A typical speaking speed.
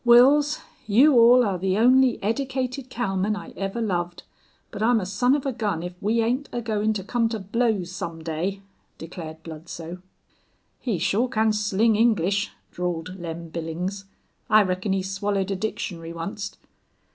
Yes: average, 160 wpm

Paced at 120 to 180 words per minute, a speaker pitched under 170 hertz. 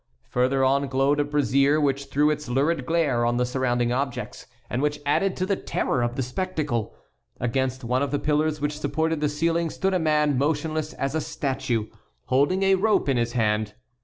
No: average, 190 wpm; medium, 140 Hz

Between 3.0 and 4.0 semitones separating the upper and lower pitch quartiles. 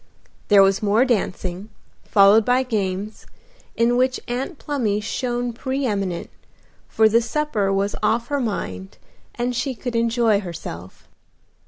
Yes: average, 3.7 semitones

